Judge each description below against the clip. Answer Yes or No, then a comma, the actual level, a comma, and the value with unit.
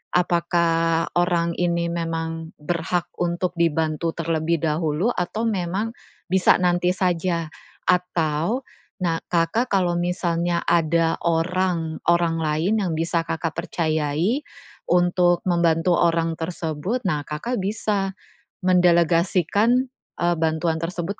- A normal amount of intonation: No, narrow, 1.6 semitones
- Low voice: No, medium, 170 Hz